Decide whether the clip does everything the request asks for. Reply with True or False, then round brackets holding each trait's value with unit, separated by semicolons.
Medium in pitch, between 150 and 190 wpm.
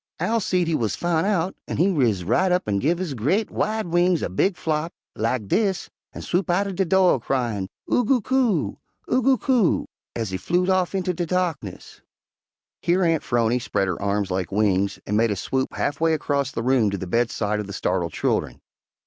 False (155 Hz; 200 wpm)